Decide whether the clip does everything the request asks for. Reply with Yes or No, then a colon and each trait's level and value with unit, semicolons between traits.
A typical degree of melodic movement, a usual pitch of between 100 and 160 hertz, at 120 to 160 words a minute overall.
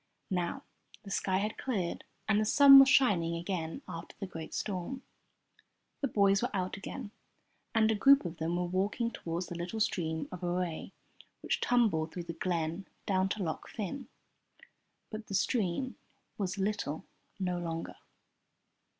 No: average, 3.9 semitones; high, 190 Hz; average, 155 wpm